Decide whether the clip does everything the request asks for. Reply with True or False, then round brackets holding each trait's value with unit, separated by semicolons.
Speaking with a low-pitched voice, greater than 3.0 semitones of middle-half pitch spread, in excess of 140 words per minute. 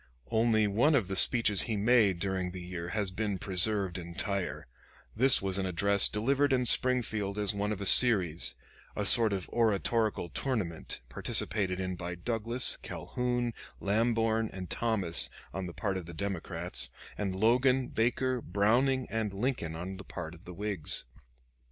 True (100 Hz; 3.9 semitones; 155 wpm)